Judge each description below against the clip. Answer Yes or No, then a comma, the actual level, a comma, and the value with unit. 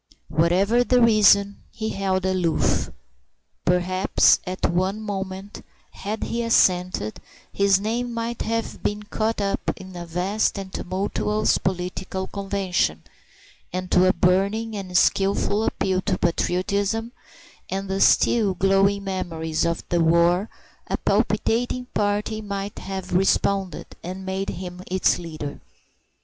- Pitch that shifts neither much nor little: No, narrow, 2.2 semitones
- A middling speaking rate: No, slow, 125 wpm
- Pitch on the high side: Yes, high, 195 Hz